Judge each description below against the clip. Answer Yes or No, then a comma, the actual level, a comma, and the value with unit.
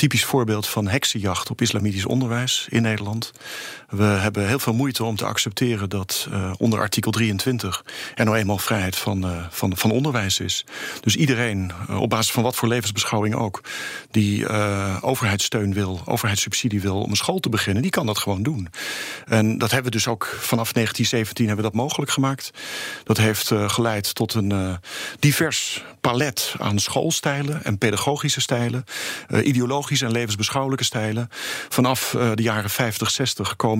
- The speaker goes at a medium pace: Yes, average, 175 wpm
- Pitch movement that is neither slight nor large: Yes, average, 3.1 semitones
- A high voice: No, low, 110 Hz